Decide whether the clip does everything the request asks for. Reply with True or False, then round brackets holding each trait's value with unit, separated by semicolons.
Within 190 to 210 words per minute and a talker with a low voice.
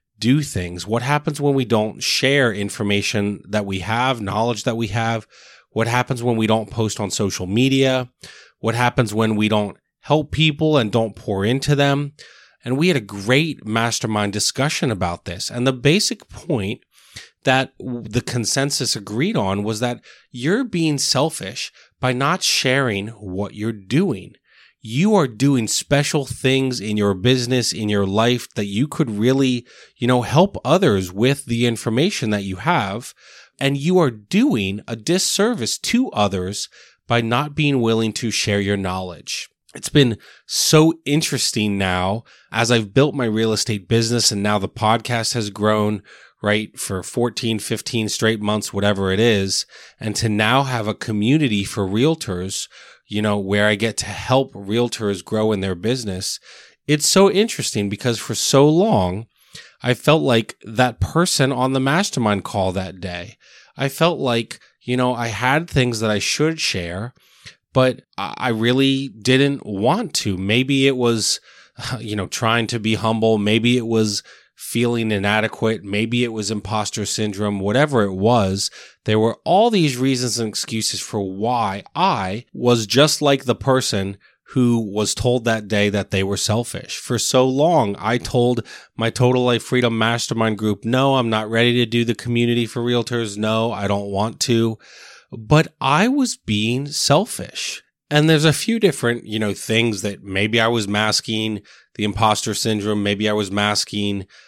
False (165 wpm; 115 Hz)